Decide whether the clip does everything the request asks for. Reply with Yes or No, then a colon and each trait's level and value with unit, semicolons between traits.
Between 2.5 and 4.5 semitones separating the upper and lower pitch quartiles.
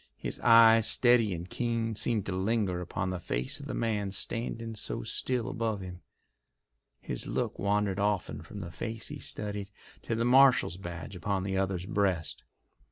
Yes: average, 3.5 semitones